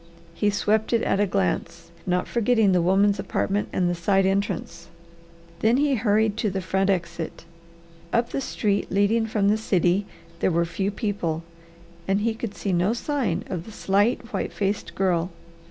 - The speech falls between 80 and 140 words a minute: No, average, 170 wpm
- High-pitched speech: Yes, high, 200 Hz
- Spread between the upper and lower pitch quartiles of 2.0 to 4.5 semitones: Yes, average, 3.3 semitones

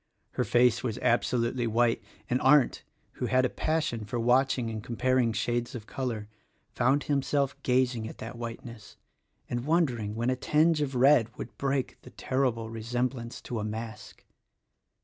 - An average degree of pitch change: No, narrow, 2.3 semitones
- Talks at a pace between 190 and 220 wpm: No, average, 165 wpm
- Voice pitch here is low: Yes, low, 120 Hz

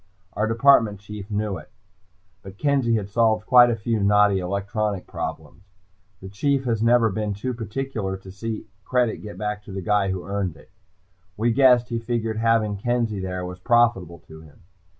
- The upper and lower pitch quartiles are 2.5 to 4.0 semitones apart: Yes, average, 3.2 semitones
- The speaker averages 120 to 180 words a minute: Yes, average, 175 wpm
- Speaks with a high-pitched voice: No, low, 105 Hz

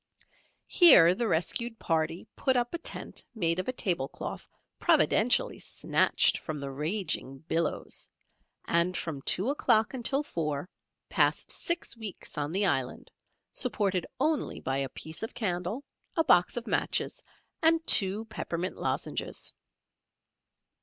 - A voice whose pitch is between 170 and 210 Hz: Yes, medium, 185 Hz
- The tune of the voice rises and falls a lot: Yes, wide, 6.8 semitones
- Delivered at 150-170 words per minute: No, slow, 135 wpm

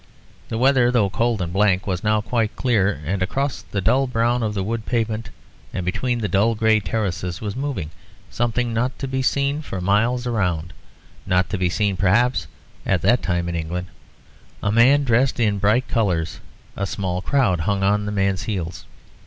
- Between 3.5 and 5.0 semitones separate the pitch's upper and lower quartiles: Yes, average, 4.3 semitones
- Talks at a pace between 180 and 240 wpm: Yes, average, 185 wpm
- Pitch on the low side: Yes, low, 105 Hz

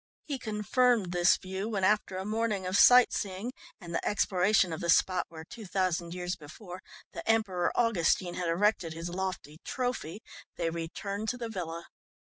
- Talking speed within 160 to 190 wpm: Yes, average, 170 wpm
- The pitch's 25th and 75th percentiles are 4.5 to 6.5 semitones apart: No, average, 3.7 semitones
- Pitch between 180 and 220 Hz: Yes, high, 190 Hz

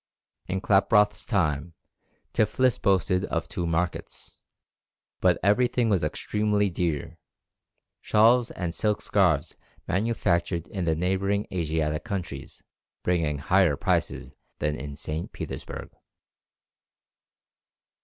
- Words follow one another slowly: Yes, slow, 100 wpm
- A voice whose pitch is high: No, very low, 90 Hz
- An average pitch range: Yes, average, 4.2 semitones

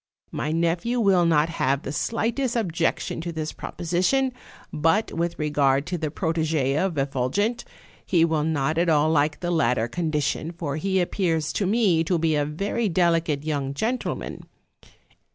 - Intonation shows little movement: No, average, 3.4 semitones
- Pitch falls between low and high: Yes, medium, 165 Hz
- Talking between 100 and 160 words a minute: Yes, average, 155 wpm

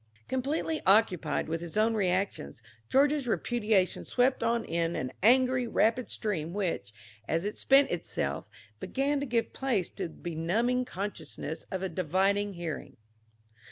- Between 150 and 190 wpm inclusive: No, average, 140 wpm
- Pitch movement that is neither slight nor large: No, wide, 6.4 semitones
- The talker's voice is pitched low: No, high, 205 Hz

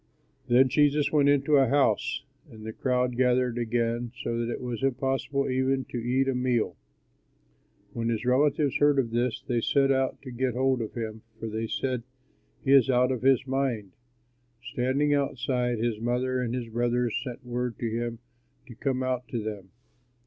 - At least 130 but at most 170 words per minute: No, average, 180 wpm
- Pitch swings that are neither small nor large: No, narrow, 2.1 semitones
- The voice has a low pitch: Yes, low, 125 Hz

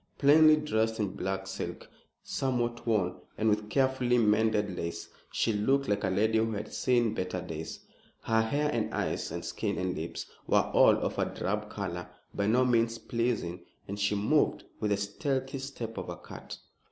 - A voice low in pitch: Yes, low, 110 Hz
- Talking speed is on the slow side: No, average, 175 wpm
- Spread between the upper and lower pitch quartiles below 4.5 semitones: Yes, average, 3.6 semitones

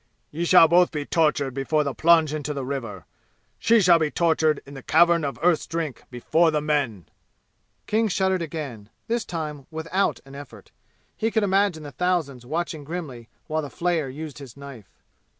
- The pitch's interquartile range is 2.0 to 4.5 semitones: Yes, average, 3.7 semitones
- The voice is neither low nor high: Yes, medium, 155 Hz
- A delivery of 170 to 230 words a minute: Yes, average, 175 wpm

